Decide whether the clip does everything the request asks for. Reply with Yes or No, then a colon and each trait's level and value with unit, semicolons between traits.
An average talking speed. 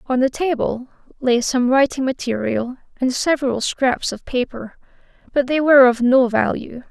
Yes: average, 155 wpm